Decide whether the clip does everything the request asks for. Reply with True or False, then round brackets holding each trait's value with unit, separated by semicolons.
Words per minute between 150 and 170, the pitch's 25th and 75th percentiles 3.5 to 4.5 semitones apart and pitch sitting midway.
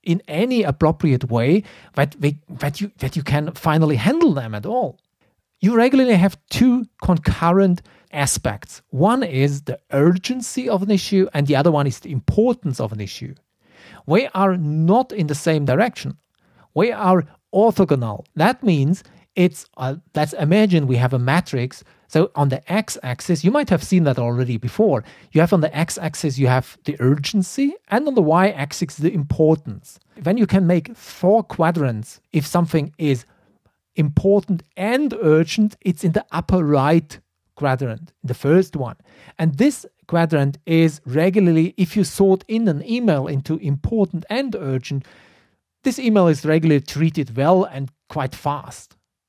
False (160 wpm; 5.5 semitones; 160 Hz)